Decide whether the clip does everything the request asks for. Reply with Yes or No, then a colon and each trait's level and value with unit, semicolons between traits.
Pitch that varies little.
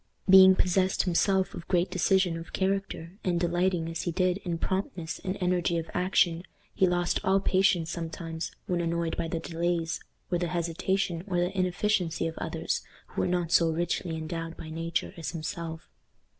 Yes: narrow, 1.9 semitones